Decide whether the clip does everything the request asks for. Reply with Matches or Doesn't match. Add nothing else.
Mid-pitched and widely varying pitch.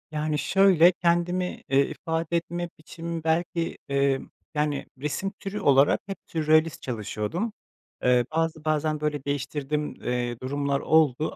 Doesn't match